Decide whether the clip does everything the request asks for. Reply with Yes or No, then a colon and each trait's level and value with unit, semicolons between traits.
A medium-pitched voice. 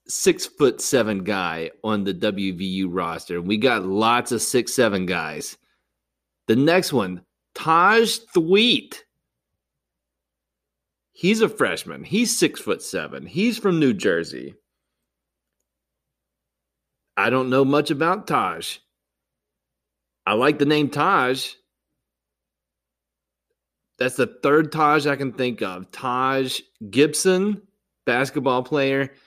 No: low, 110 Hz